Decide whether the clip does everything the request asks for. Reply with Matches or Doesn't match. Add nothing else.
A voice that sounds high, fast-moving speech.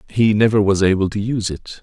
Doesn't match